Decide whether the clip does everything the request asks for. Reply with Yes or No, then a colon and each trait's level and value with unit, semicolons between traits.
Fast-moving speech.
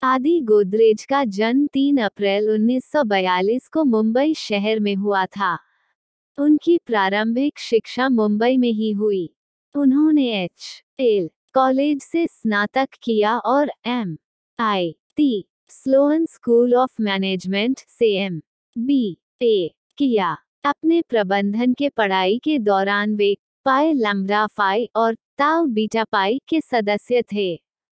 No: average, 115 wpm